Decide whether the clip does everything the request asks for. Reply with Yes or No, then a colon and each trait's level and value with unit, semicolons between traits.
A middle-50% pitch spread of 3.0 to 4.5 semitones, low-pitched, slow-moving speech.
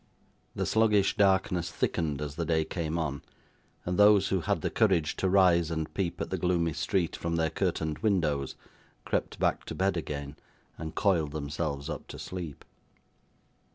No: average, 3.5 semitones; very low, 85 Hz; average, 165 wpm